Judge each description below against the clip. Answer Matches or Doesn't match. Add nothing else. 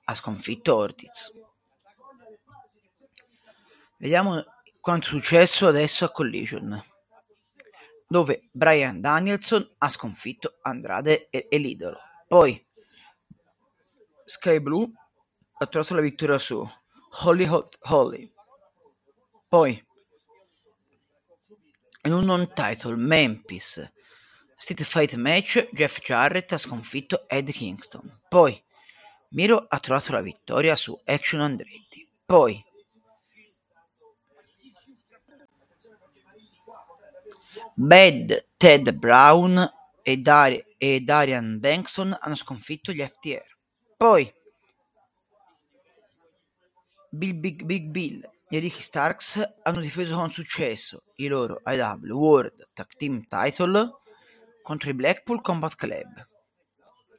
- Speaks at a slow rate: Matches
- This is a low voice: Doesn't match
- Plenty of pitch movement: Matches